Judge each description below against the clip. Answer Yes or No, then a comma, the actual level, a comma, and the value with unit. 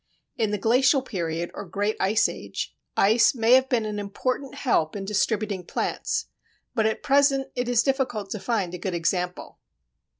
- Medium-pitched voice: No, high, 220 Hz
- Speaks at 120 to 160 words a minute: No, average, 170 wpm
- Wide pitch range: No, average, 4.5 semitones